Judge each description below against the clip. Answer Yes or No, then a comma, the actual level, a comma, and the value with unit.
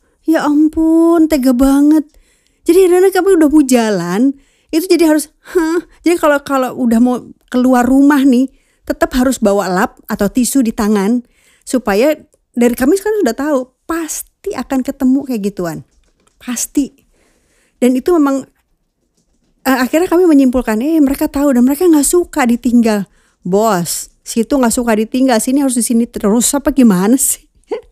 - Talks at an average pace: No, fast, 150 wpm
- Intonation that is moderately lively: Yes, average, 4.2 semitones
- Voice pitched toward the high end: Yes, very high, 270 Hz